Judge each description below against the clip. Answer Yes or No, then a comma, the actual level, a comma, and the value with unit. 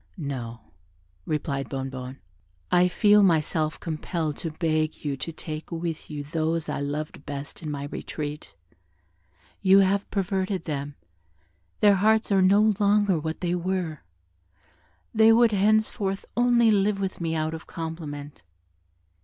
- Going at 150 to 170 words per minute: No, slow, 135 wpm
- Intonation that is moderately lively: Yes, average, 4.6 semitones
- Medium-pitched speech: Yes, medium, 165 Hz